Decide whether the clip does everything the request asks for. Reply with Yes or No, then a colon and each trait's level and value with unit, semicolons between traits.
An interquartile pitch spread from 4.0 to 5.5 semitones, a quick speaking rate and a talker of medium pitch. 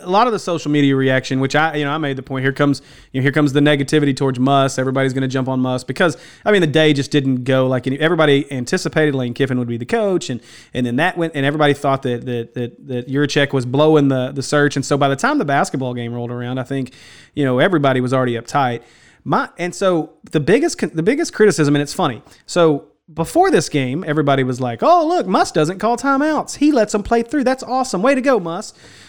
Yes: average, 4.4 semitones; fast, 250 wpm; medium, 145 Hz